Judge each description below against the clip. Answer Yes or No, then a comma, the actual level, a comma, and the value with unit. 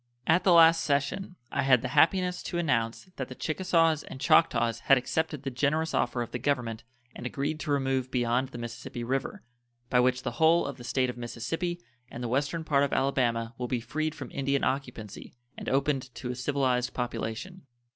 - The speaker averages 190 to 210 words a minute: Yes, average, 195 wpm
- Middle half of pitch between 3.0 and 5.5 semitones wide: Yes, average, 4.1 semitones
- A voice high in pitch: No, low, 135 Hz